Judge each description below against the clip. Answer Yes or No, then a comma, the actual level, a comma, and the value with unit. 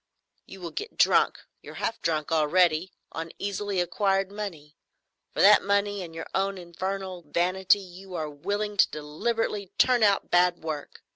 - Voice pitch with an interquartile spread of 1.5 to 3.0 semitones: No, average, 3.5 semitones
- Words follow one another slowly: No, average, 145 wpm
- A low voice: No, medium, 185 Hz